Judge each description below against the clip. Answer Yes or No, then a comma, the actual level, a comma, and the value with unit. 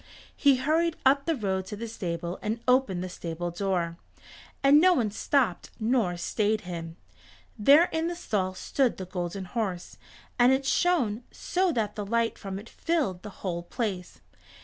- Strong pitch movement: Yes, wide, 6.4 semitones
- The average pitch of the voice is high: Yes, high, 215 Hz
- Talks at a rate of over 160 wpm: Yes, average, 170 wpm